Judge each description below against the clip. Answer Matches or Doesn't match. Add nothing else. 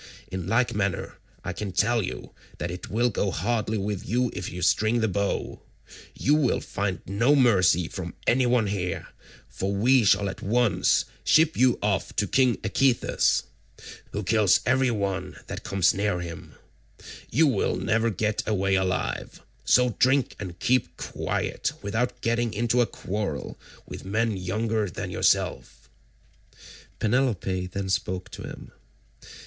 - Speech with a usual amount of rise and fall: Matches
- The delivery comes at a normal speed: Matches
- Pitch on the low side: Matches